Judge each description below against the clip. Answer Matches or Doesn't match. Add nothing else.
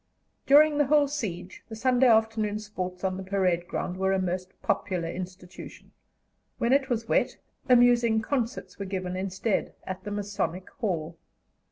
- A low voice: Doesn't match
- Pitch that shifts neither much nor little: Matches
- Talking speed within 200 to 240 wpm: Doesn't match